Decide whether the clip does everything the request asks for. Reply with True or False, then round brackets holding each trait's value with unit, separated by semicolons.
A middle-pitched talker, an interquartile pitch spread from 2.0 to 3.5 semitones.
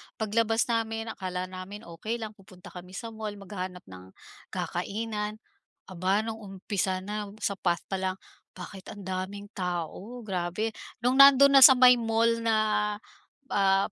False (205 Hz; 3.2 semitones)